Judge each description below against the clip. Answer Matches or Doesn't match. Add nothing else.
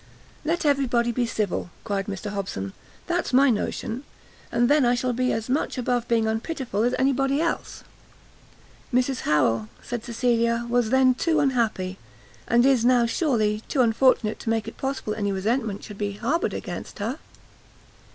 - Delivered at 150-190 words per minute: Matches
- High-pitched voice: Matches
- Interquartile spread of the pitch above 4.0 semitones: Doesn't match